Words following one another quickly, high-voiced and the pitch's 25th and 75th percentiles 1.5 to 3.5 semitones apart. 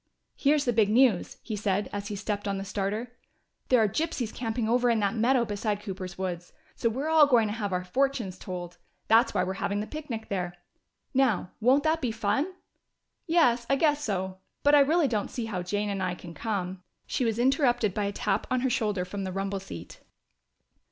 No: fast, 210 wpm; high, 215 Hz; average, 4.4 semitones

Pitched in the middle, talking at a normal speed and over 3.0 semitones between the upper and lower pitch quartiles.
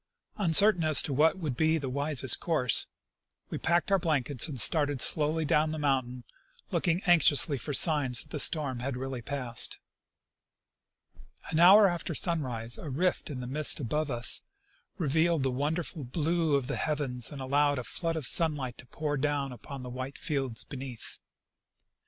Yes: medium, 145 Hz; average, 170 wpm; average, 3.6 semitones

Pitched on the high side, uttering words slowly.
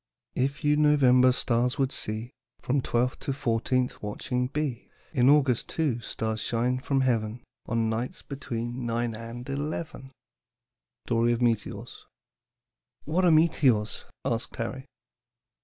No: low, 125 Hz; slow, 125 wpm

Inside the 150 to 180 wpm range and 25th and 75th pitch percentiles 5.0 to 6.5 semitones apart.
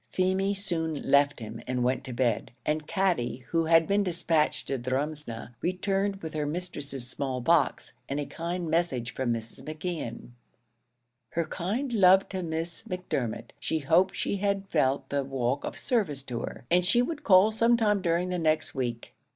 Yes: average, 175 wpm; wide, 5.6 semitones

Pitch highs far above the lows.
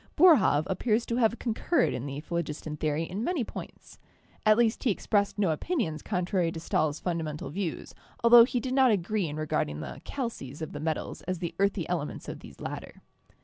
Yes: wide, 6.9 semitones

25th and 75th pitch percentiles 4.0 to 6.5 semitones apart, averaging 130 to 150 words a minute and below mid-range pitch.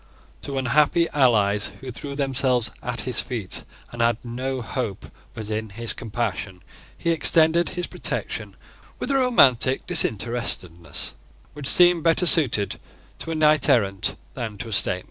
Yes: wide, 5.5 semitones; average, 145 wpm; low, 125 Hz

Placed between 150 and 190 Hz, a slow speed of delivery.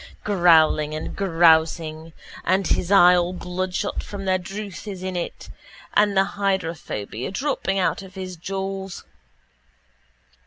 Yes: medium, 185 Hz; slow, 125 wpm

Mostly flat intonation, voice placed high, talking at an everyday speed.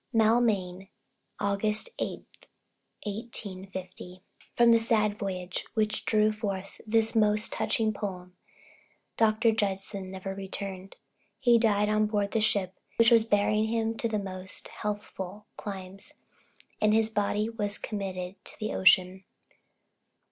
No: narrow, 2.3 semitones; high, 210 Hz; slow, 120 wpm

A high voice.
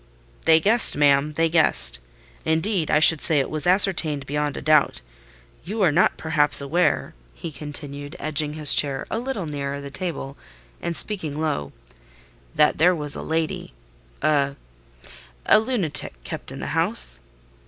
No: medium, 150 Hz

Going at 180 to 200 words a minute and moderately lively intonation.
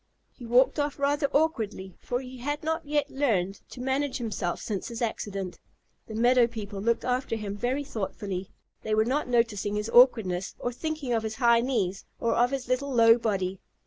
Yes: average, 185 wpm; average, 4.1 semitones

